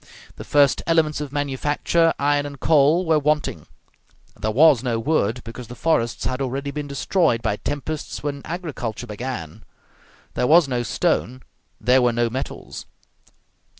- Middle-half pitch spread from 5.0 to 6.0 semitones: No, average, 3.8 semitones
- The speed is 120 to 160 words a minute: Yes, average, 150 wpm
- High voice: No, medium, 140 Hz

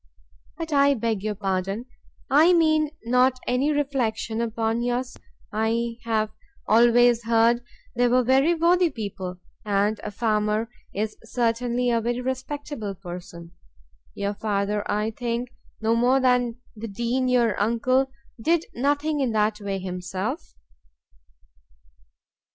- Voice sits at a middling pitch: No, high, 235 Hz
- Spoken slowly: Yes, slow, 125 wpm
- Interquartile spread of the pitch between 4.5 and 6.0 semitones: No, average, 3.3 semitones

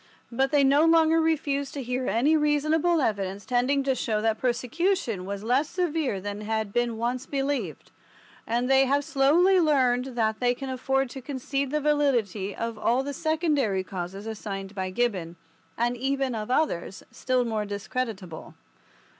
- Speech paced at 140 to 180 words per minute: Yes, average, 160 wpm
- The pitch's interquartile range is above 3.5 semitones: Yes, average, 4.7 semitones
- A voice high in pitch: Yes, very high, 255 Hz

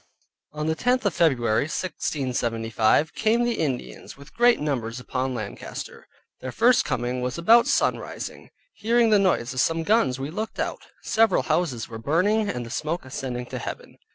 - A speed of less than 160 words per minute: No, average, 165 wpm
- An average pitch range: No, wide, 8.9 semitones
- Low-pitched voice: No, medium, 150 Hz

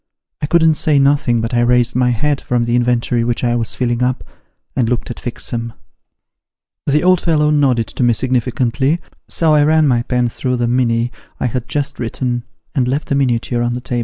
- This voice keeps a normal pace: No, fast, 210 wpm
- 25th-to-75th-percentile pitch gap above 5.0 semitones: No, average, 2.9 semitones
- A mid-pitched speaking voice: No, low, 125 Hz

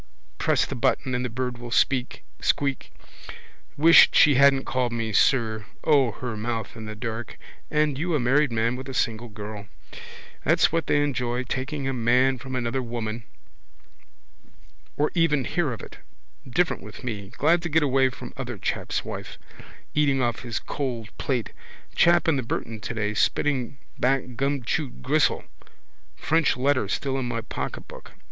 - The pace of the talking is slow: No, average, 160 wpm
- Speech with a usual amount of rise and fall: Yes, average, 3.2 semitones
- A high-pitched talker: No, low, 125 Hz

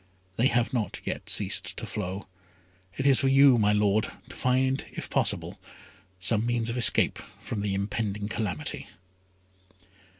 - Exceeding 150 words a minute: No, average, 145 wpm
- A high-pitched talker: No, low, 110 Hz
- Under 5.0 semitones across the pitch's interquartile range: Yes, average, 3.6 semitones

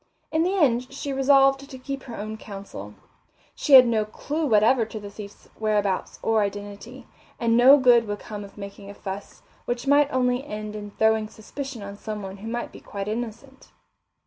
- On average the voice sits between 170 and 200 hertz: No, high, 225 Hz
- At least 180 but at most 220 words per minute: Yes, average, 185 wpm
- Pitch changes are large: No, average, 4.3 semitones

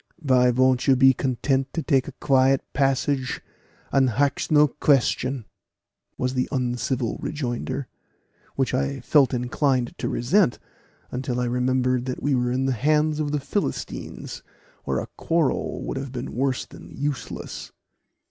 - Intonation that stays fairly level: Yes, narrow, 1.9 semitones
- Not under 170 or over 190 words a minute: No, average, 150 wpm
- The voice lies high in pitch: No, low, 130 Hz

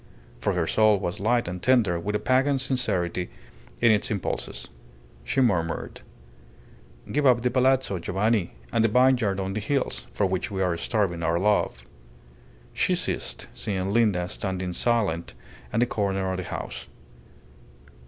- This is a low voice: Yes, low, 100 Hz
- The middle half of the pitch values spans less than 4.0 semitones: No, average, 4.8 semitones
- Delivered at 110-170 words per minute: Yes, average, 155 wpm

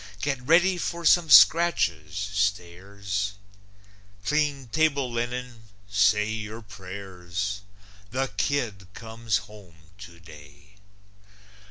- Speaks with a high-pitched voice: No, low, 105 Hz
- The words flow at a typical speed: No, slow, 85 wpm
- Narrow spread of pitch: No, average, 4.7 semitones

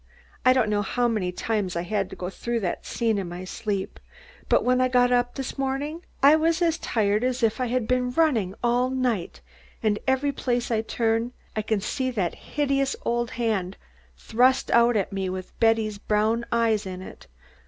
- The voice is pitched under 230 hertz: No, high, 235 Hz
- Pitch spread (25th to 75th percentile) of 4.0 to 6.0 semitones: No, average, 3.5 semitones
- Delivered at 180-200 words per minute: Yes, average, 195 wpm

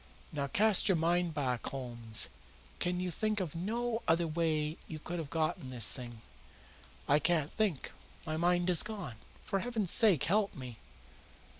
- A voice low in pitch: No, medium, 165 Hz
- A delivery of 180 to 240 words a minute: No, average, 160 wpm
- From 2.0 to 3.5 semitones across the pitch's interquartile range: No, average, 5.3 semitones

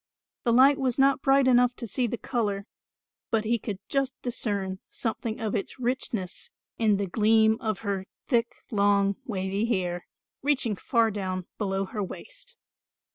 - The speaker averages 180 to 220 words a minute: No, average, 155 wpm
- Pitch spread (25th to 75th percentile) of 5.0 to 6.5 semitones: No, average, 3.8 semitones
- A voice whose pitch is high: Yes, high, 220 Hz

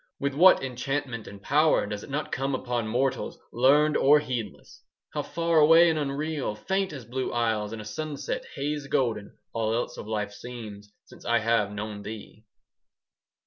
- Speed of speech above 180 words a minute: No, average, 175 wpm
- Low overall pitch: Yes, low, 125 Hz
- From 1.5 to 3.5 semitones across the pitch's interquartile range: No, average, 5.2 semitones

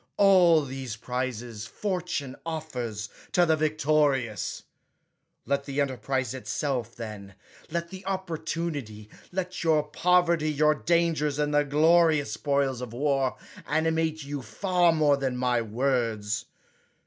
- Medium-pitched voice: Yes, medium, 145 Hz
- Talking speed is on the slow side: Yes, slow, 120 wpm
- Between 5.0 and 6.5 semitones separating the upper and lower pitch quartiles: No, average, 4.5 semitones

